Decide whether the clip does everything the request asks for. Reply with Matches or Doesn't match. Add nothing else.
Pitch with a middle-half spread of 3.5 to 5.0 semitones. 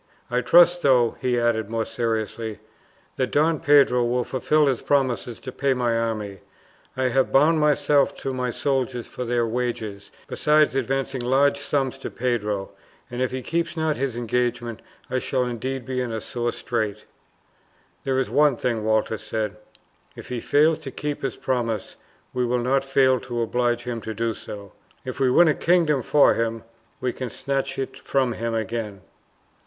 Doesn't match